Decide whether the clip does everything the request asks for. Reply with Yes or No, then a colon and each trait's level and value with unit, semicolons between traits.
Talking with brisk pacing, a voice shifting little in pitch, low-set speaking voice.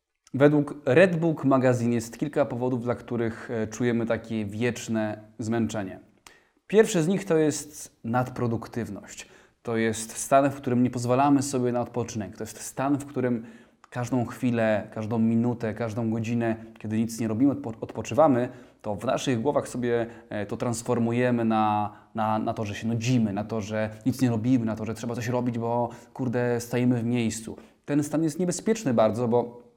Yes: fast, 165 wpm; narrow, 2.1 semitones; low, 120 Hz